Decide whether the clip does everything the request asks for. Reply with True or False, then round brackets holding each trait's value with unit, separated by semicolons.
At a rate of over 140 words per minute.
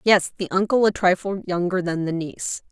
True (200 wpm)